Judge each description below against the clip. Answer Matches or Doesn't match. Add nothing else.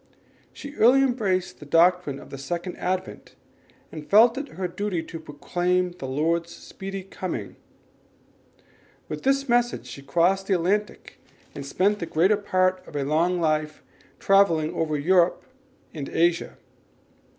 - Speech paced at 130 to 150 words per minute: Matches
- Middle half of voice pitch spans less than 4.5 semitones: Matches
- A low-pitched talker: Doesn't match